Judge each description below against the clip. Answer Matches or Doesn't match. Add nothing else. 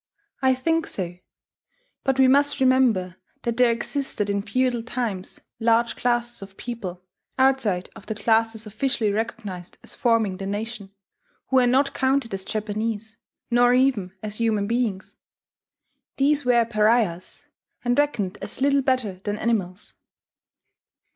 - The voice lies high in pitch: Matches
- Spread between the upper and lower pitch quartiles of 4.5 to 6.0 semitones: Doesn't match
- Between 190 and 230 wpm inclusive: Doesn't match